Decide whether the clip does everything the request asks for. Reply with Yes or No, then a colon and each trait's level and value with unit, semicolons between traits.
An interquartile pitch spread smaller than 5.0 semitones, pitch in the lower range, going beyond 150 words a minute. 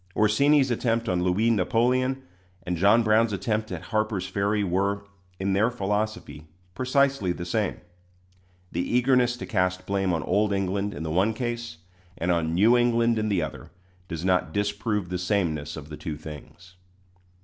Yes: average, 4.2 semitones; low, 100 Hz; average, 160 wpm